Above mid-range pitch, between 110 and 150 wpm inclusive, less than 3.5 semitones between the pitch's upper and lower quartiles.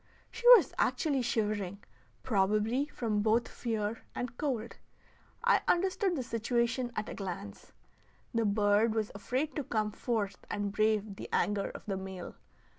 Yes: high, 220 Hz; average, 145 wpm; average, 3.1 semitones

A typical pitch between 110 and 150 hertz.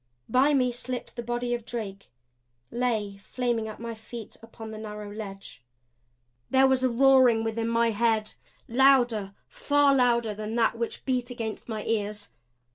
No: high, 230 Hz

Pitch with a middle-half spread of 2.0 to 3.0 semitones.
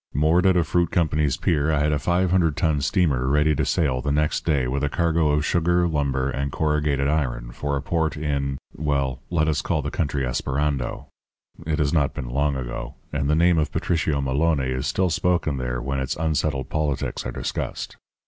Yes: average, 2.7 semitones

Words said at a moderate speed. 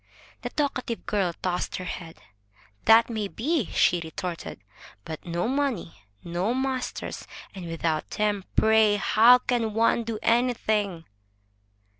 No: slow, 125 wpm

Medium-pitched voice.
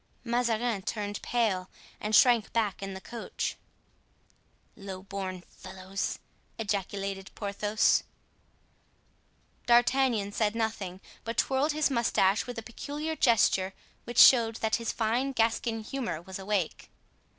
No: high, 220 Hz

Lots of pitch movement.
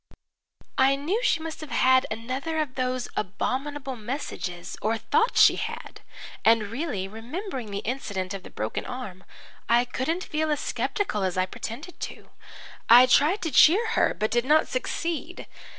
Yes: wide, 6.0 semitones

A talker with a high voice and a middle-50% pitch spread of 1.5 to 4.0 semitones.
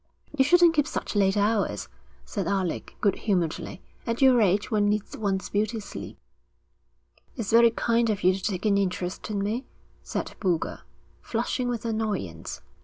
Yes: high, 210 Hz; average, 3.1 semitones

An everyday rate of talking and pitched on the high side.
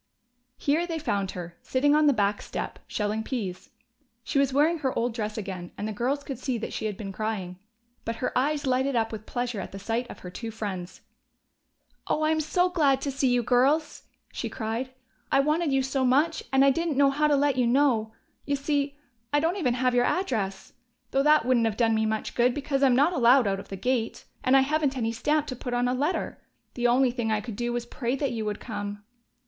No: fast, 230 wpm; very high, 250 Hz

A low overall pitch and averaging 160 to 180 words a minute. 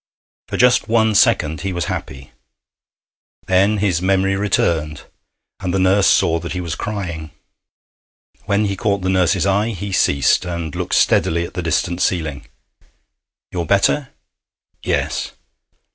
No: very low, 95 Hz; average, 140 wpm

